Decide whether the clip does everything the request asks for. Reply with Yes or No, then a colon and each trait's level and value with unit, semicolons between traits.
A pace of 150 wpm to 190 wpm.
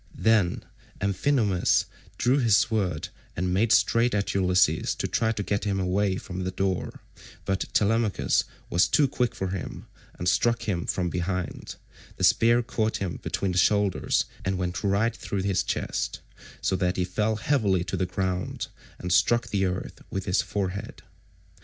Yes: average, 165 wpm